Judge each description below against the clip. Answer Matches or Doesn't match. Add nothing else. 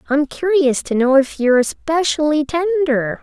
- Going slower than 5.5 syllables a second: Matches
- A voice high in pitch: Matches